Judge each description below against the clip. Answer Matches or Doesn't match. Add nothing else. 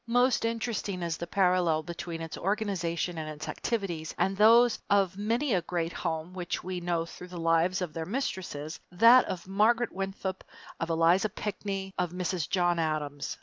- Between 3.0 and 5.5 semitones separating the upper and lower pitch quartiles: Matches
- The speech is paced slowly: Doesn't match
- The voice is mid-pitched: Matches